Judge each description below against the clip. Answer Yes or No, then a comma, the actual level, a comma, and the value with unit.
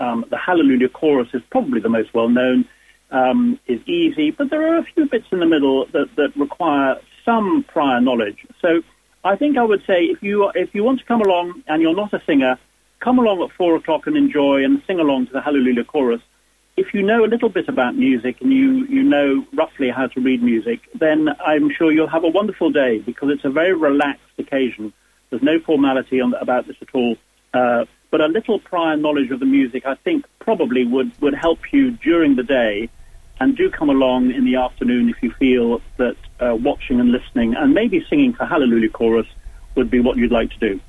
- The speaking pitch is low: No, medium, 155 Hz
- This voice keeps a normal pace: No, fast, 215 wpm